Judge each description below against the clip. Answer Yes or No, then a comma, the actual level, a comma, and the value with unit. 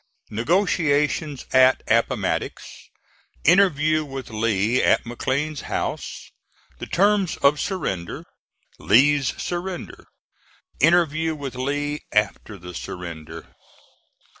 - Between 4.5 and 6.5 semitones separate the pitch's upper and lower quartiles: Yes, wide, 5.4 semitones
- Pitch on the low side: No, medium, 145 Hz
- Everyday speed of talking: No, slow, 90 wpm